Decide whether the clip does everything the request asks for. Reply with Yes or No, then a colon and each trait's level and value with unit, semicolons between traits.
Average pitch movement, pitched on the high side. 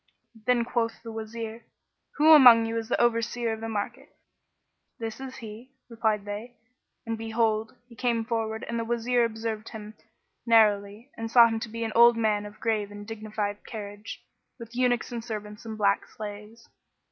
No: narrow, 1.4 semitones; high, 225 Hz